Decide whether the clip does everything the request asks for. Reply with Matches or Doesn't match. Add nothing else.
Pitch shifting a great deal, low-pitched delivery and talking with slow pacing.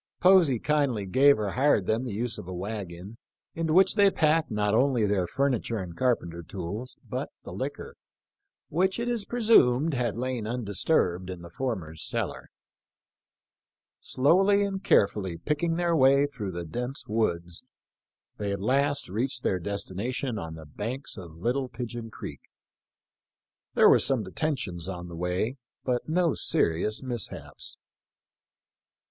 Doesn't match